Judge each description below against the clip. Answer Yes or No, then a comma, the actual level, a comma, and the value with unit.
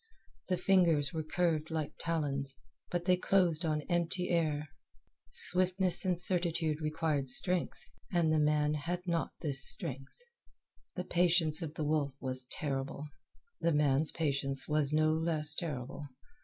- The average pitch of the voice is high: No, medium, 155 Hz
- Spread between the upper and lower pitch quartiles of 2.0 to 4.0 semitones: Yes, average, 2.8 semitones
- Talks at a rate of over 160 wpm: No, average, 140 wpm